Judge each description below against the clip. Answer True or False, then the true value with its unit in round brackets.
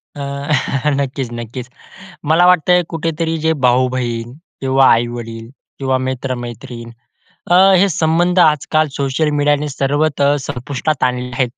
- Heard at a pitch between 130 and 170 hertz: True (135 Hz)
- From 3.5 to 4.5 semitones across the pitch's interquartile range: True (4.1 semitones)